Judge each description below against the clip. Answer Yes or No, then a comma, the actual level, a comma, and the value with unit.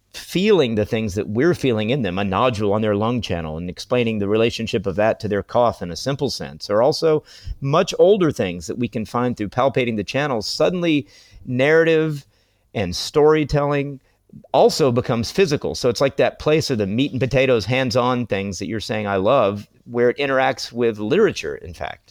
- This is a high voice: No, low, 120 Hz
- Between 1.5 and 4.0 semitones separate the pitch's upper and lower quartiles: No, average, 4.6 semitones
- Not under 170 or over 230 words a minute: Yes, average, 195 wpm